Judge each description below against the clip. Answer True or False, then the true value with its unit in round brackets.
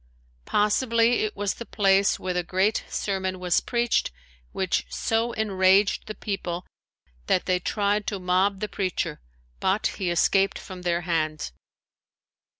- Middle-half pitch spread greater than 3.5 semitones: False (2.5 semitones)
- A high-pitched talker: True (195 Hz)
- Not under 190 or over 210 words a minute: False (140 wpm)